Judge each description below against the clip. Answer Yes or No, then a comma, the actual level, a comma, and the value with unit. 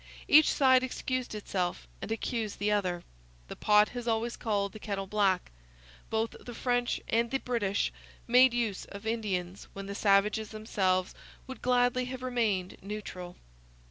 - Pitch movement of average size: Yes, average, 3.6 semitones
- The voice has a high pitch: Yes, high, 215 Hz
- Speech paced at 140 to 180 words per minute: Yes, average, 150 wpm